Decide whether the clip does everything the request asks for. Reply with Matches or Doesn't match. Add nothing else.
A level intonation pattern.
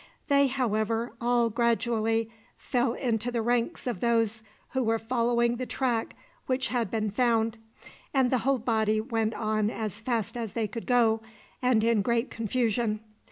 Matches